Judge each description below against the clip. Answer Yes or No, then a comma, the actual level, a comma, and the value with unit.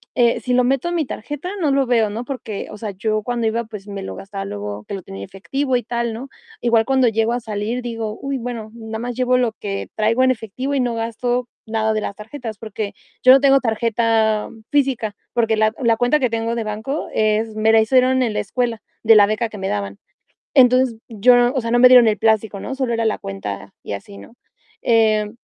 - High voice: Yes, high, 225 Hz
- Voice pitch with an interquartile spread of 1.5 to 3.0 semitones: Yes, narrow, 2.6 semitones